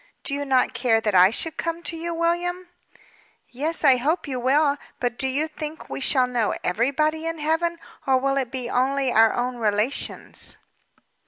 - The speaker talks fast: No, average, 180 wpm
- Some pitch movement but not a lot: Yes, average, 4.4 semitones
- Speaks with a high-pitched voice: Yes, very high, 275 Hz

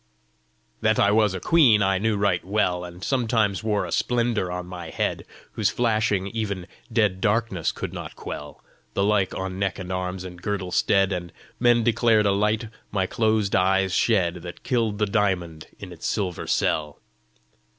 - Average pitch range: Yes, average, 3.1 semitones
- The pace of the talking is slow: No, average, 170 wpm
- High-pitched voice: No, low, 100 Hz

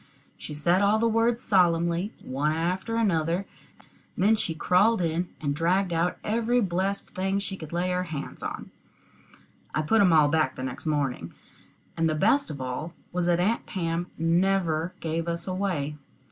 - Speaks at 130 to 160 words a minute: No, average, 175 wpm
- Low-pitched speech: No, medium, 175 Hz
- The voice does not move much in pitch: No, average, 3.5 semitones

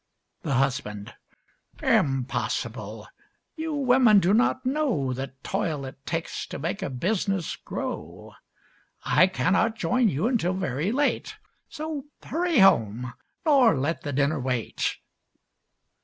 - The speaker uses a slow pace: Yes, slow, 120 wpm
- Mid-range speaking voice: Yes, medium, 180 Hz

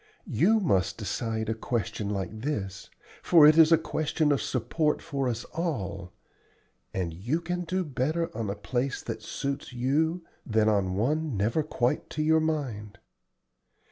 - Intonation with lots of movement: Yes, wide, 6.6 semitones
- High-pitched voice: No, low, 130 Hz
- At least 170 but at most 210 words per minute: No, average, 155 wpm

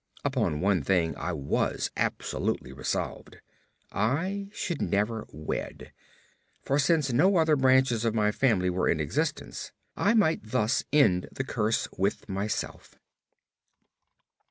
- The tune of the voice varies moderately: No, wide, 7.4 semitones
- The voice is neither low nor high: No, low, 110 Hz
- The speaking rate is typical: No, slow, 125 wpm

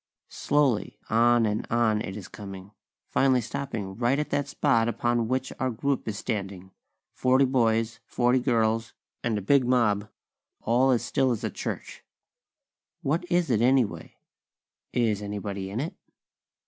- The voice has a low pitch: Yes, low, 120 Hz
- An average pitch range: Yes, average, 3.6 semitones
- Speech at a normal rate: Yes, average, 145 wpm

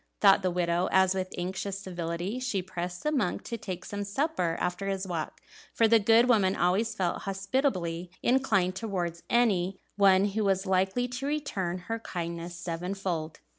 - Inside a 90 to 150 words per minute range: No, average, 165 wpm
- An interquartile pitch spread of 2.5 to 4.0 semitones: Yes, average, 3.6 semitones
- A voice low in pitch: No, high, 190 Hz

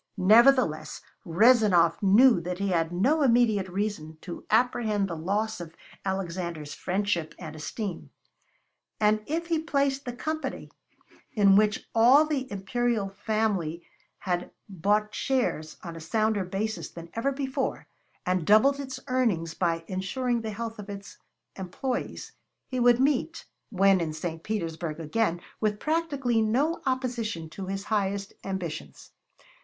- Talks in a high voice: Yes, high, 205 Hz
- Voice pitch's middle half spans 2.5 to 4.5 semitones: No, wide, 5.5 semitones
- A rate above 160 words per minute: No, slow, 135 wpm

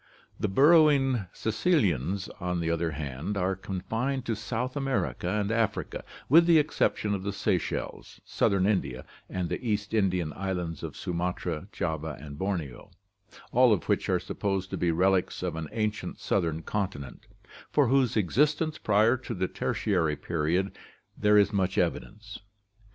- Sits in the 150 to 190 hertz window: No, very low, 95 Hz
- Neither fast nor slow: Yes, average, 150 wpm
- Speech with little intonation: No, average, 4.5 semitones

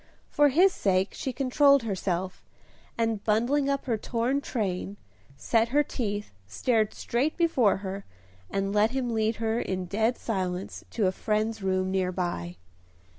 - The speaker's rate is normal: Yes, average, 150 wpm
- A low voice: No, high, 220 Hz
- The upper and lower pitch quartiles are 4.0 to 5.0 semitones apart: Yes, average, 4.5 semitones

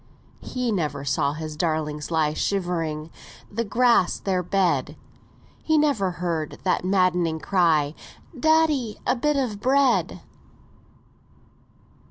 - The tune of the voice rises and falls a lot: Yes, wide, 7.0 semitones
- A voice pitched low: No, medium, 180 Hz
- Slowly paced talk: Yes, slow, 110 wpm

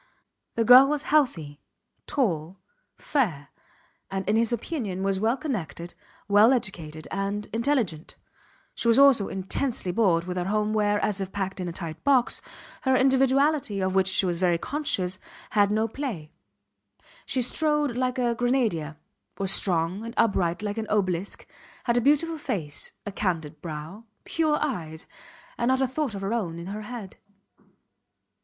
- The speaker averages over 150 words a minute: Yes, average, 160 wpm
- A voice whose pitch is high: Yes, high, 210 Hz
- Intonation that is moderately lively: No, wide, 5.7 semitones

